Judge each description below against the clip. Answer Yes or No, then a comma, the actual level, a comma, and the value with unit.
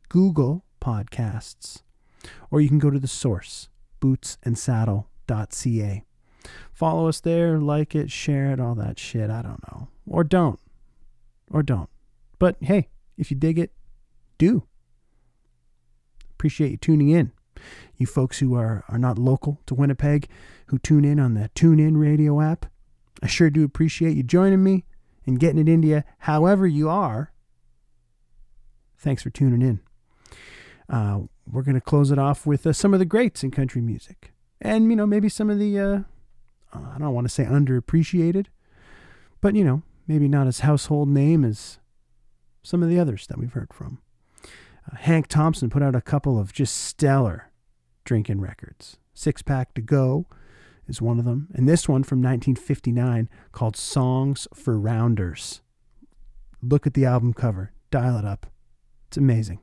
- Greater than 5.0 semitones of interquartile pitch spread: Yes, wide, 5.4 semitones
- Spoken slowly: No, average, 160 wpm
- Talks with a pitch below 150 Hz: Yes, low, 135 Hz